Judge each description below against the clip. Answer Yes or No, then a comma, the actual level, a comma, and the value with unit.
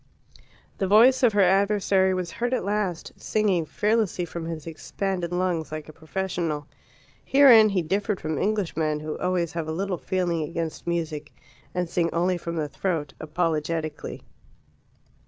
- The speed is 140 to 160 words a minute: Yes, average, 150 wpm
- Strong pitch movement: No, average, 3.5 semitones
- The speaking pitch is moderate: Yes, medium, 175 Hz